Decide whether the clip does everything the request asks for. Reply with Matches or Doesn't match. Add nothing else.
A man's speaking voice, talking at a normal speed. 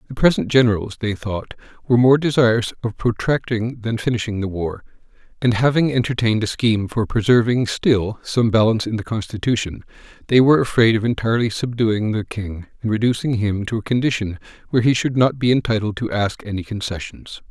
Matches